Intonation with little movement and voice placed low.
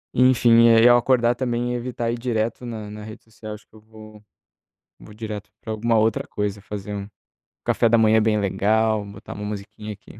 Yes: narrow, 1.9 semitones; low, 110 Hz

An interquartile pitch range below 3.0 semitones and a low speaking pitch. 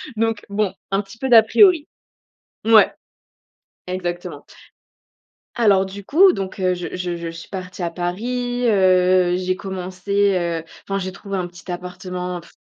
No: narrow, 2.5 semitones; medium, 185 Hz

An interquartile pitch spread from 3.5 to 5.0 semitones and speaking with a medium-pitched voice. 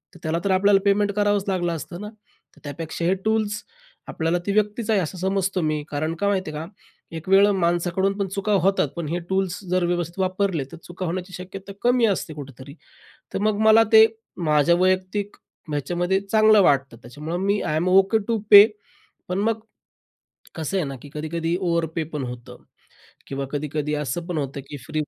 Yes: average, 4.1 semitones; medium, 180 Hz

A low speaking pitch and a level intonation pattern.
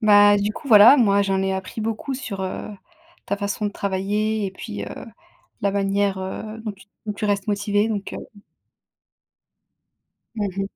No: high, 205 Hz; narrow, 1.5 semitones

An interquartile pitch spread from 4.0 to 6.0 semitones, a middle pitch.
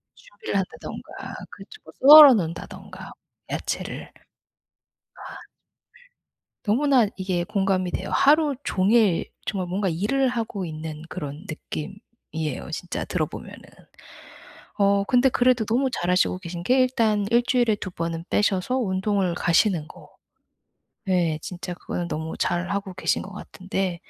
No: average, 5.2 semitones; high, 195 Hz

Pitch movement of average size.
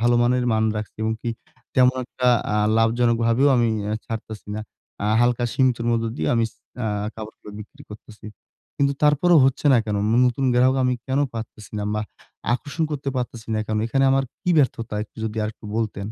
Yes: average, 3.0 semitones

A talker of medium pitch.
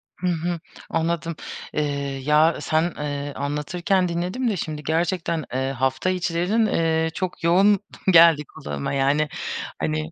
Yes: medium, 160 Hz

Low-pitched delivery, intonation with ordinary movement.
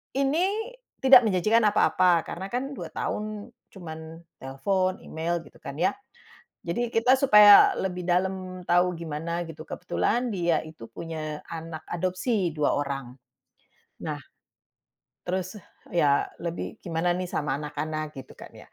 No: medium, 175 Hz; average, 4.4 semitones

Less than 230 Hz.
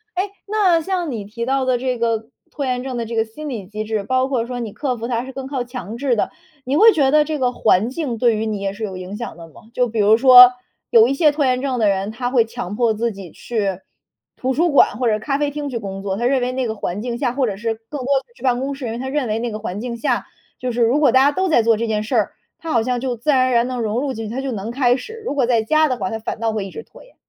No: high, 245 Hz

